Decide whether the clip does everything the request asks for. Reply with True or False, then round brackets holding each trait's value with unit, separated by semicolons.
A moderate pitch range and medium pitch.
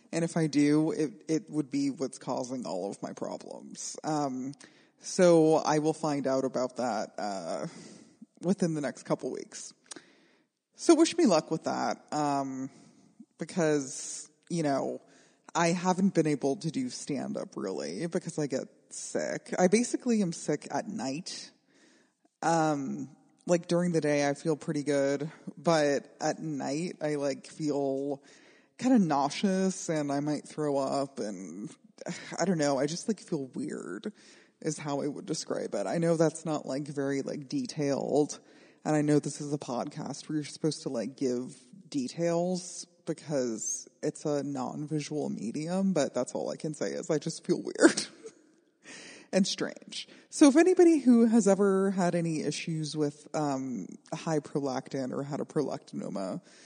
True (4.6 semitones; 155 Hz)